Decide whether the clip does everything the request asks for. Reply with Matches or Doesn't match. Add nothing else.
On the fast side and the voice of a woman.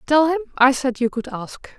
Matches